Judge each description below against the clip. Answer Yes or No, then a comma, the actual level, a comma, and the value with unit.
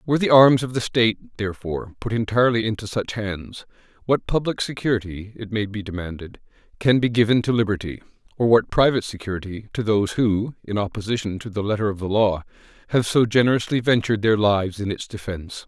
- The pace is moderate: Yes, average, 185 wpm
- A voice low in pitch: Yes, low, 110 Hz